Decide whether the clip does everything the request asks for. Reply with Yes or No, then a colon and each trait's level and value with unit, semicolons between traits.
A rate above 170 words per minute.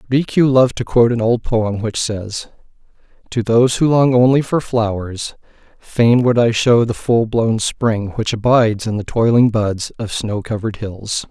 Yes: average, 180 wpm